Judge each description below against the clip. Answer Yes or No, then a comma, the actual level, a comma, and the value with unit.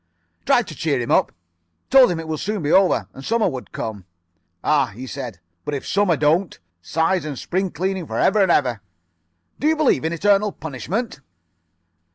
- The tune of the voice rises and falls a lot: Yes, wide, 6.4 semitones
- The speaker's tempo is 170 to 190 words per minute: Yes, average, 185 wpm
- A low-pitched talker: No, medium, 165 Hz